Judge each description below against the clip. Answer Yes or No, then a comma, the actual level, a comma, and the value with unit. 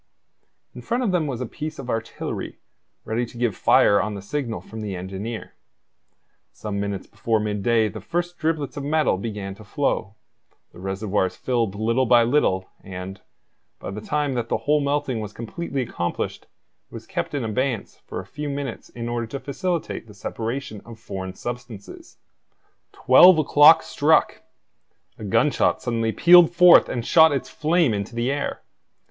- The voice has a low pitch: Yes, low, 120 Hz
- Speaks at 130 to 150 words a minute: No, average, 165 wpm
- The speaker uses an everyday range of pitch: No, wide, 5.7 semitones